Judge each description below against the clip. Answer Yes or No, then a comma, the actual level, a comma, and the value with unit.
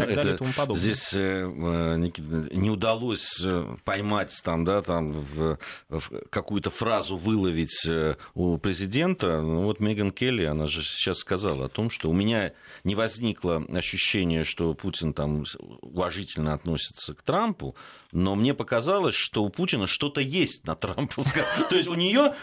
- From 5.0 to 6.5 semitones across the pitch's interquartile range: Yes, average, 5.3 semitones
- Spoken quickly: No, average, 145 wpm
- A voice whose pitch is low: Yes, very low, 95 Hz